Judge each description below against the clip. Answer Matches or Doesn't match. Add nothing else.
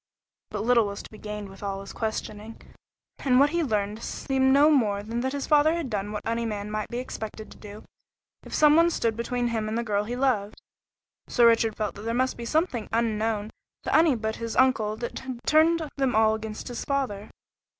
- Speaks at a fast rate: Matches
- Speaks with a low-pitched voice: Doesn't match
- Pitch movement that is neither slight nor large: Matches